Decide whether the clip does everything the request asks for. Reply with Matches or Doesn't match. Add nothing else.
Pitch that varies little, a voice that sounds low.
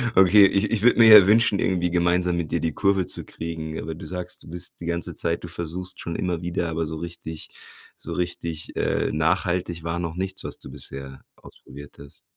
Matches